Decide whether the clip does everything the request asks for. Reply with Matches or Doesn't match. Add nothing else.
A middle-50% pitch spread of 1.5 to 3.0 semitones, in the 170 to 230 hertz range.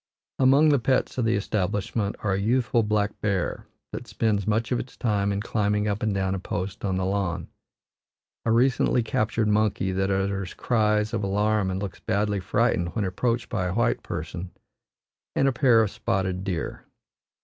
Doesn't match